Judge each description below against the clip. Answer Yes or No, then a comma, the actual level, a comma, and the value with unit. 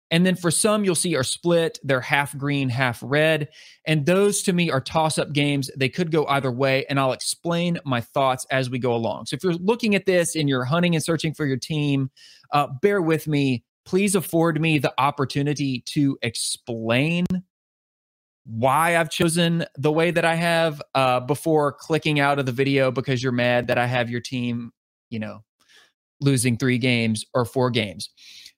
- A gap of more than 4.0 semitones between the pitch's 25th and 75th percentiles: Yes, average, 4.4 semitones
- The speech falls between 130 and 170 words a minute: No, average, 190 wpm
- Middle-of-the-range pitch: Yes, medium, 145 Hz